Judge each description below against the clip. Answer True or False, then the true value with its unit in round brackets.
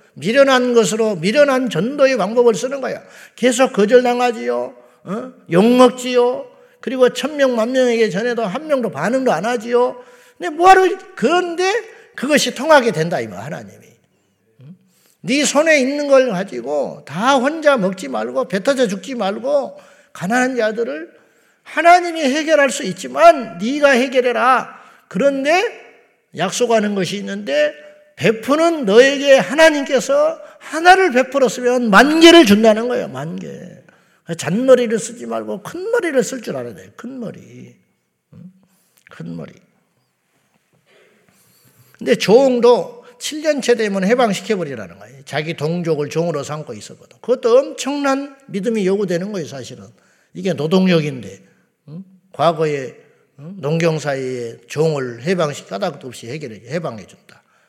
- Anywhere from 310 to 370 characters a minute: False (285 characters per minute)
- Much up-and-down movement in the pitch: True (7.3 semitones)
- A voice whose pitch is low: False (245 Hz)